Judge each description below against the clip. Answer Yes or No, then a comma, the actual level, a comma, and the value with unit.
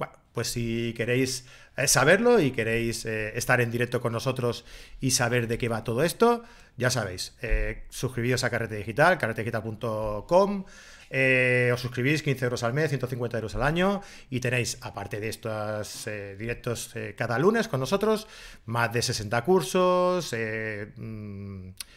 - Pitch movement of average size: Yes, average, 3.2 semitones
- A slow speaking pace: No, average, 155 wpm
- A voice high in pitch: No, low, 120 Hz